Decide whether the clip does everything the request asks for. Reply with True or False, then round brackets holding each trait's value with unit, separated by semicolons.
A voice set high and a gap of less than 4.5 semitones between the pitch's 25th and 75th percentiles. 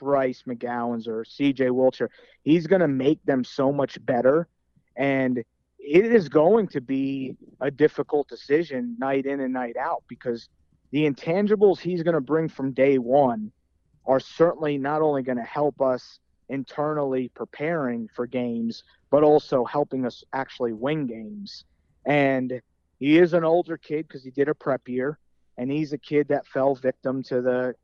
False (135 Hz; 3.1 semitones)